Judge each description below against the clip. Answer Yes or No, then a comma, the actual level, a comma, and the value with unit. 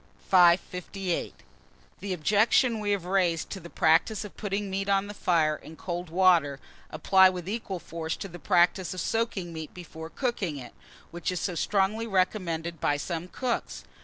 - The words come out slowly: No, average, 165 wpm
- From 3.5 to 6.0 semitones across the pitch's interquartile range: No, average, 3.0 semitones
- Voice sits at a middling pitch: Yes, medium, 180 Hz